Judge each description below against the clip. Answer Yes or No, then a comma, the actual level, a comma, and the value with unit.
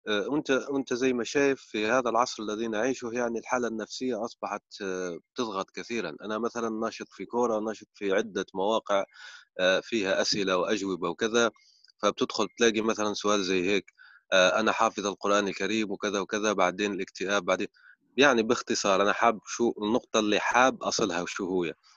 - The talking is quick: Yes, fast, 150 wpm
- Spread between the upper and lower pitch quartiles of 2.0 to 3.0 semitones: Yes, narrow, 2.6 semitones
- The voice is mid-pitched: No, low, 110 Hz